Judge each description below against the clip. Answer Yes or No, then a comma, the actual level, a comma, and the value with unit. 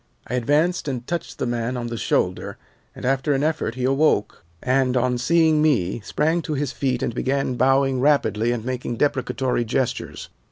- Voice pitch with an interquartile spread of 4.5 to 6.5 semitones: No, average, 3.2 semitones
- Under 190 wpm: Yes, average, 175 wpm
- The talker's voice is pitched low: Yes, low, 130 Hz